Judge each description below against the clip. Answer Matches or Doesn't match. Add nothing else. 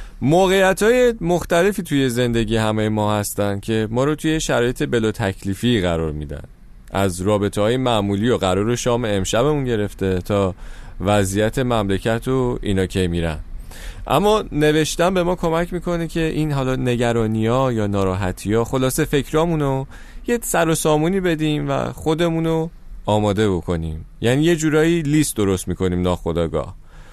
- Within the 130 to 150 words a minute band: Matches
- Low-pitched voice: Matches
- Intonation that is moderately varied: Doesn't match